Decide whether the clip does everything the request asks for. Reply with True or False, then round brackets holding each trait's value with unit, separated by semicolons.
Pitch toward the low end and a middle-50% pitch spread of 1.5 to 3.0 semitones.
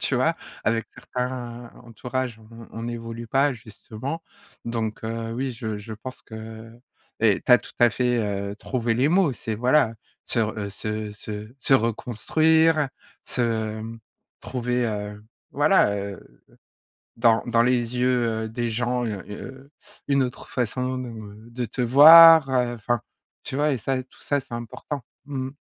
True (120 Hz; 2.7 semitones)